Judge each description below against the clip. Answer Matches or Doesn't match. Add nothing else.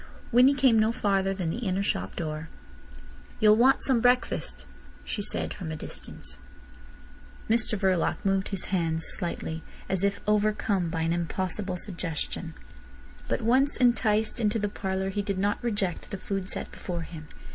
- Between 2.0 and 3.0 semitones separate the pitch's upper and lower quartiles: Doesn't match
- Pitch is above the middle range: Matches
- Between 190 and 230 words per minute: Doesn't match